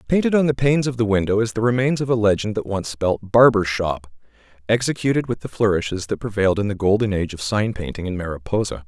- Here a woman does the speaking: No, male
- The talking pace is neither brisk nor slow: No, fast, 225 wpm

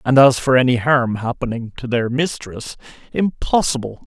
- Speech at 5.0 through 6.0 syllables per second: No, 4.8 syllables/s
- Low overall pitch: Yes, low, 125 Hz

